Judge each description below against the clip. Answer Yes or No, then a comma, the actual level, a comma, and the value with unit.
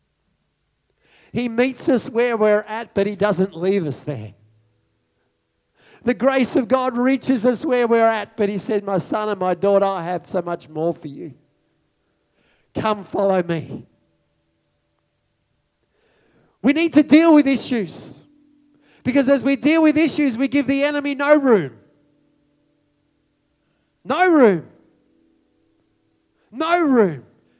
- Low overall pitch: No, high, 215 Hz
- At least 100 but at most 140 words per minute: Yes, slow, 135 wpm